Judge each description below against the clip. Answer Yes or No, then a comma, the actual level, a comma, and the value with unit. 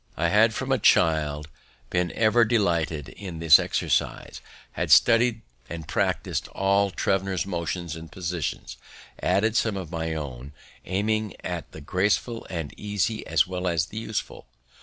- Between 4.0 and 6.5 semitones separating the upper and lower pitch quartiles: Yes, average, 4.6 semitones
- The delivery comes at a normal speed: Yes, average, 145 wpm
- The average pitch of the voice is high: No, very low, 90 Hz